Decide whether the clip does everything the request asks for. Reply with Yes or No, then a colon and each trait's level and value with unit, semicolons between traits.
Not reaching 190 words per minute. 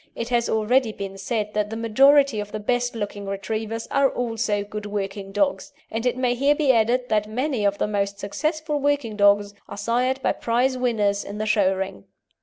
No: average, 200 wpm